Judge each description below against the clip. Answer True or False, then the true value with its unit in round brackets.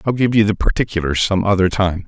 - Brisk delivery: True (230 wpm)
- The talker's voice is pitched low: True (100 Hz)